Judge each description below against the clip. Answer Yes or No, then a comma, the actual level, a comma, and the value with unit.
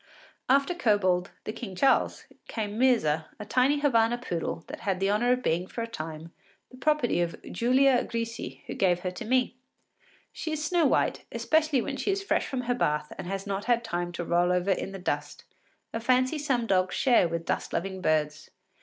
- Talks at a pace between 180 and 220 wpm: Yes, average, 200 wpm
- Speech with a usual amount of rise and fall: No, wide, 6.3 semitones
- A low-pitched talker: No, high, 220 Hz